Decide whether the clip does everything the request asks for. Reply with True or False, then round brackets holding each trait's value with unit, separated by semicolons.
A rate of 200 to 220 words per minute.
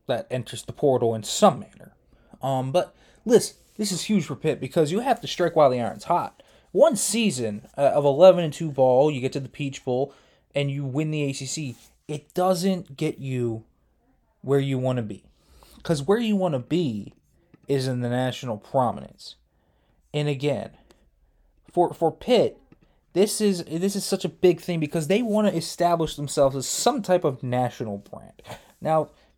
False (180 wpm)